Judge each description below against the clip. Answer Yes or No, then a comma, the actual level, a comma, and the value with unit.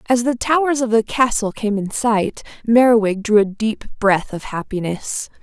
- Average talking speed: Yes, average, 175 wpm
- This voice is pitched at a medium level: No, high, 220 Hz